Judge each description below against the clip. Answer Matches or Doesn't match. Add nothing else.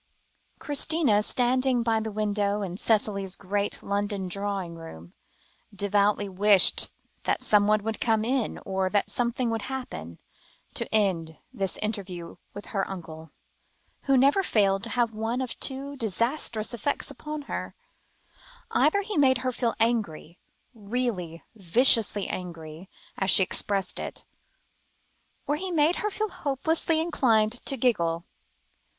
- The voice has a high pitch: Matches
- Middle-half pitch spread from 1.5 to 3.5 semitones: Doesn't match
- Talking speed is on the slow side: Matches